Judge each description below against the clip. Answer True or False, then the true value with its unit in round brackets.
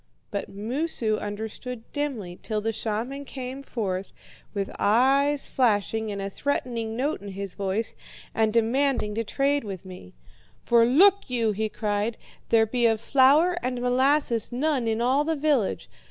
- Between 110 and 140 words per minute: False (155 wpm)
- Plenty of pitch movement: False (4.4 semitones)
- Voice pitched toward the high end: True (230 Hz)